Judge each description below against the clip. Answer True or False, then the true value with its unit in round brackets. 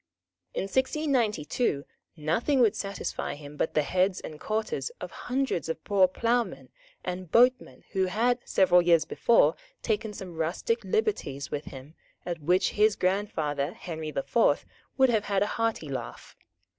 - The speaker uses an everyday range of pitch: False (6.5 semitones)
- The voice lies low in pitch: False (190 Hz)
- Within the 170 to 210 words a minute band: False (150 wpm)